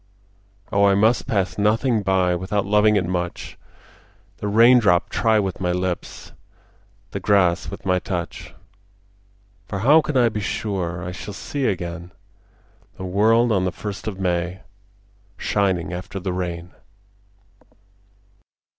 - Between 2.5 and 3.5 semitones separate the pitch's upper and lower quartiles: Yes, average, 2.9 semitones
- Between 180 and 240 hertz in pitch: No, very low, 95 Hz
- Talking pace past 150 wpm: No, slow, 135 wpm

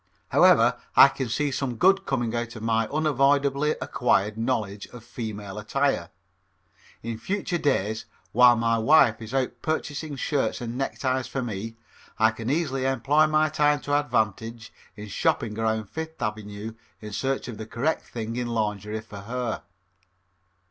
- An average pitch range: Yes, average, 4.0 semitones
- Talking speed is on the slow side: No, average, 155 wpm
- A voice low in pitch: Yes, low, 120 Hz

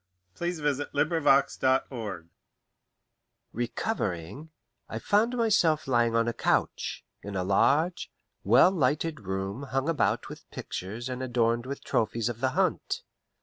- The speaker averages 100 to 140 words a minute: Yes, slow, 135 wpm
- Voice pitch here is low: Yes, low, 130 Hz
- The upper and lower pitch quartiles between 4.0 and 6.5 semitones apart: Yes, average, 5.0 semitones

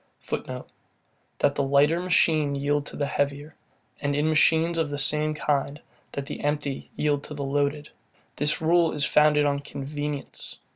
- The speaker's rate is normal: Yes, average, 160 wpm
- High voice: No, medium, 145 Hz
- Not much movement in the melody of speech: Yes, narrow, 1.3 semitones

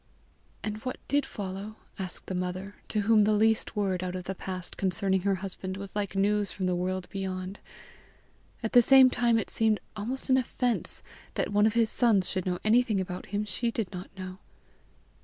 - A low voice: No, high, 200 Hz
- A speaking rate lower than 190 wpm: No, average, 195 wpm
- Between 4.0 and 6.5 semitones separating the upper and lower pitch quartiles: No, average, 2.9 semitones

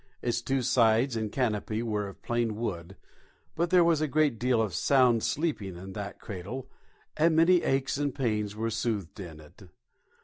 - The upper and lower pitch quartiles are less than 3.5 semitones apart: No, average, 4.5 semitones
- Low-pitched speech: Yes, low, 115 Hz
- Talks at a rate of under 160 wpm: No, average, 175 wpm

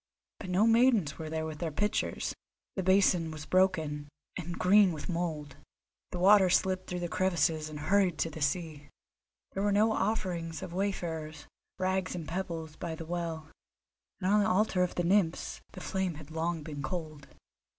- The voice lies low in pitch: No, medium, 175 Hz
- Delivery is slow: No, average, 175 wpm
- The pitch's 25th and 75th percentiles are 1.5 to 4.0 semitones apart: Yes, average, 3.1 semitones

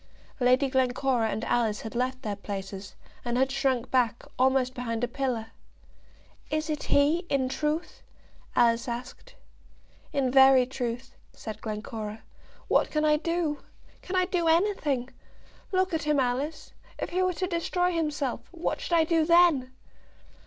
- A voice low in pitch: No, very high, 265 Hz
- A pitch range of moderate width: Yes, average, 4.7 semitones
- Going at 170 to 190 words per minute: No, average, 150 wpm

